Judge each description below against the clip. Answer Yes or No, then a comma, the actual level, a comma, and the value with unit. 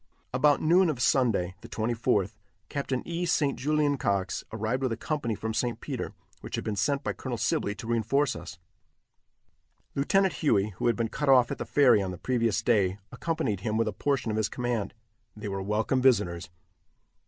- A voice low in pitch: Yes, low, 115 Hz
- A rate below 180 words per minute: No, average, 190 wpm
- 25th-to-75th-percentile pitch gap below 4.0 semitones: No, average, 4.8 semitones